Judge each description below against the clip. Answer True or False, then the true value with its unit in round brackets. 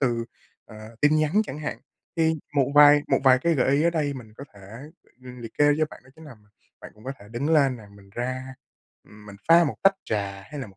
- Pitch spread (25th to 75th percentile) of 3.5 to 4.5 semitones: False (4.9 semitones)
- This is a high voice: False (130 Hz)